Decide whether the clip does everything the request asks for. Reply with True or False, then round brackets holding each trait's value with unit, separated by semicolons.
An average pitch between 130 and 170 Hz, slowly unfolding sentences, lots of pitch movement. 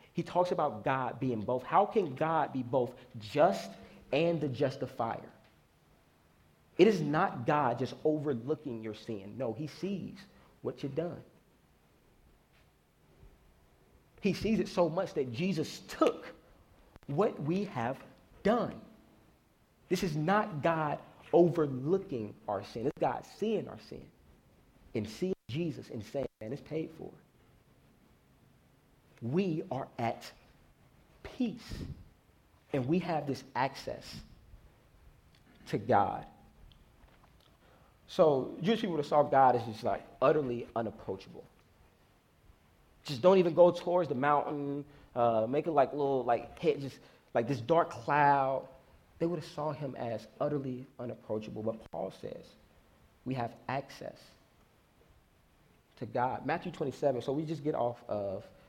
True (140 Hz; 130 wpm; 6.4 semitones)